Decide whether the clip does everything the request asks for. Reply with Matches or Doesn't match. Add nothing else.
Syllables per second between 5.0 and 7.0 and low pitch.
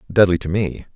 Matches